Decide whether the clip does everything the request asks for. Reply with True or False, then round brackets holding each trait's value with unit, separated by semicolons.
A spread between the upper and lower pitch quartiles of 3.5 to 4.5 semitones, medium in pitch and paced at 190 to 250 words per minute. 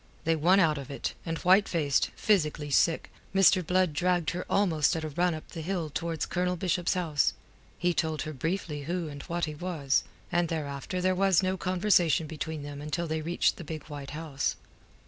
False (3.0 semitones; 165 Hz; 195 wpm)